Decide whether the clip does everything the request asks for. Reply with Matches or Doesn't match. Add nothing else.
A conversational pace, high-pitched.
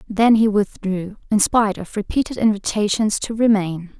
Matches